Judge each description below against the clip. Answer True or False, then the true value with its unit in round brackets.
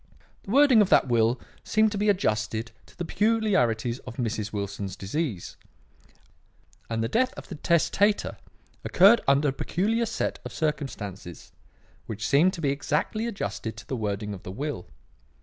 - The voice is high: False (135 Hz)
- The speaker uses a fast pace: False (160 wpm)